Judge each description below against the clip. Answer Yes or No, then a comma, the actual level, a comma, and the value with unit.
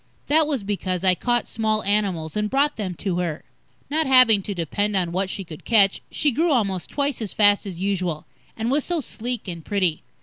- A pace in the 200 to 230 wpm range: Yes, fast, 205 wpm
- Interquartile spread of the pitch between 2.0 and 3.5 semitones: No, average, 4.9 semitones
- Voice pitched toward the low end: No, high, 205 Hz